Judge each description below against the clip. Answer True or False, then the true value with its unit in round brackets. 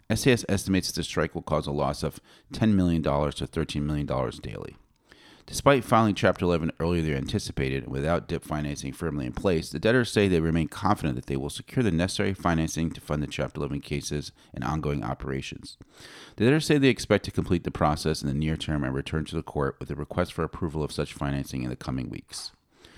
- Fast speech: True (215 wpm)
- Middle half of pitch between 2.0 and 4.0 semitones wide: False (4.7 semitones)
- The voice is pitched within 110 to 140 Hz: False (80 Hz)